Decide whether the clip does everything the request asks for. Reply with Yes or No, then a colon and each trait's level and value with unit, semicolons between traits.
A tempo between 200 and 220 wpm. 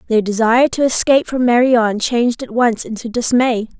No: average, 175 wpm